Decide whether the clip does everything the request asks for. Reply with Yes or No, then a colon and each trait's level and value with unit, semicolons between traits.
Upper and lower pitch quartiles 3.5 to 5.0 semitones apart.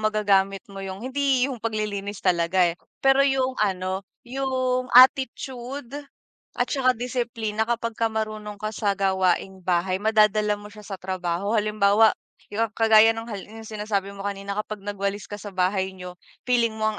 No: average, 2.9 semitones